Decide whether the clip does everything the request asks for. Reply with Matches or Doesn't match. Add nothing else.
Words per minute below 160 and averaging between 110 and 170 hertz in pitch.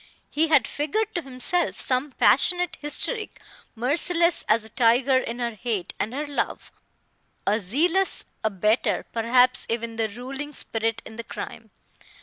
Doesn't match